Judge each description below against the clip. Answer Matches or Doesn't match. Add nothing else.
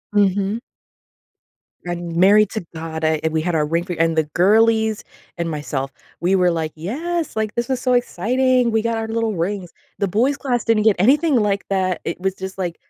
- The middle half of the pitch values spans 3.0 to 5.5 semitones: Matches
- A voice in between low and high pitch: Doesn't match